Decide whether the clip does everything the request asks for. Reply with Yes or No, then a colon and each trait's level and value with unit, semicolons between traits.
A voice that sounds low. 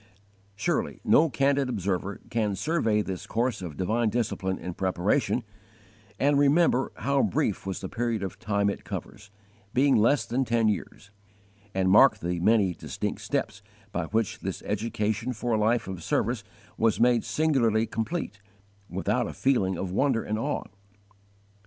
Yes: low, 110 Hz